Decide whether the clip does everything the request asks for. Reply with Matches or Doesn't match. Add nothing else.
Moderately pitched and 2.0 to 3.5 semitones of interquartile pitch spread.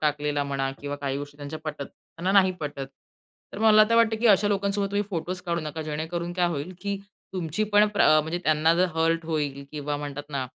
Doesn't match